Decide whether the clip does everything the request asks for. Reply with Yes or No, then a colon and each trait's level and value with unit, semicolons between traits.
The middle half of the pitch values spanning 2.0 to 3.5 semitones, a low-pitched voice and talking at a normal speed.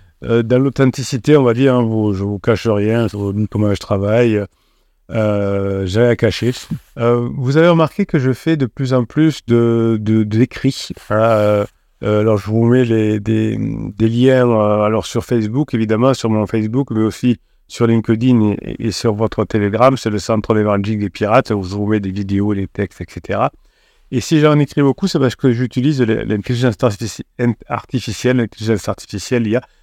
Yes: average, 3.2 semitones; low, 115 Hz; average, 195 wpm